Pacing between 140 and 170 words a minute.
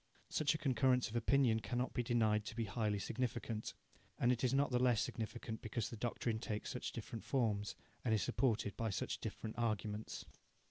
No: average, 180 wpm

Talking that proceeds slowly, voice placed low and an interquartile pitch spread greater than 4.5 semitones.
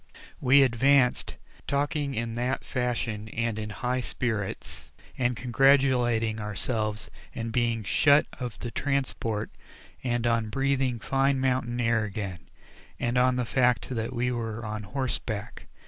No: slow, 130 wpm; low, 120 Hz; average, 2.7 semitones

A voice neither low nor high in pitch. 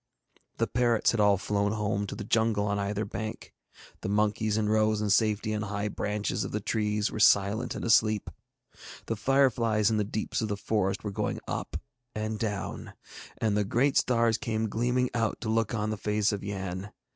No: low, 105 Hz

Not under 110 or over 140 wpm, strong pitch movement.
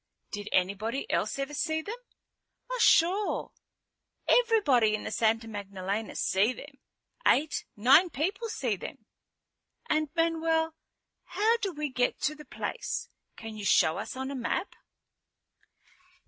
Yes: slow, 135 wpm; wide, 7.0 semitones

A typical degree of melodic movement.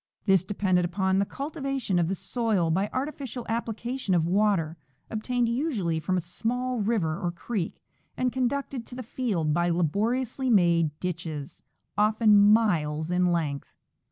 No: wide, 5.7 semitones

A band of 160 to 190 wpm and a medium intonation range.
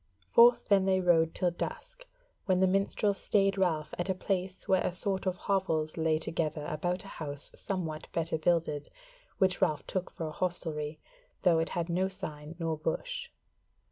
Yes: average, 175 wpm; average, 3.2 semitones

